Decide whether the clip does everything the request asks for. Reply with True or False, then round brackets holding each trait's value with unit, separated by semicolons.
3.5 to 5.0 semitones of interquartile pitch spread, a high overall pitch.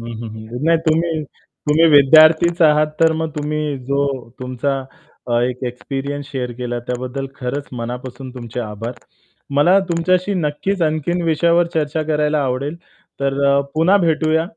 False (4.0 semitones; 145 Hz)